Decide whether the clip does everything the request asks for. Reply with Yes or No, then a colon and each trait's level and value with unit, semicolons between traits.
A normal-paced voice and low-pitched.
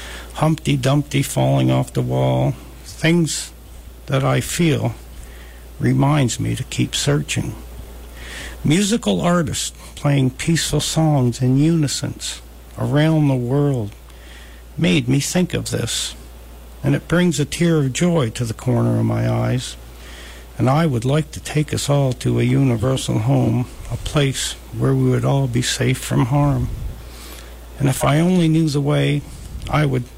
Yes: average, 145 wpm; low, 125 Hz